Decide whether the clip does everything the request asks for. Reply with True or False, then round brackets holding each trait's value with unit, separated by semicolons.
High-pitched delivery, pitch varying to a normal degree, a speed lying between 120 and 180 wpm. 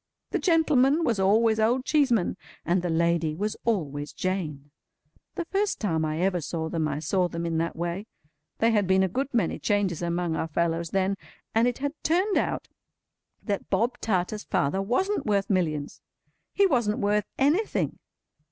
False (195 Hz; 5.9 semitones; 170 wpm)